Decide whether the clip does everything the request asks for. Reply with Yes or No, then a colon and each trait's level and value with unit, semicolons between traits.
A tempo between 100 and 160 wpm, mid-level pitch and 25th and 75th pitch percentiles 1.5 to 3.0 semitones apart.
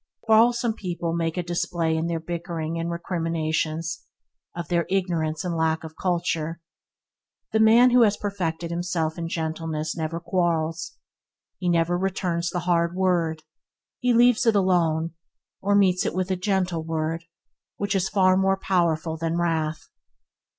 Yes: average, 150 wpm; medium, 170 Hz; narrow, 2.4 semitones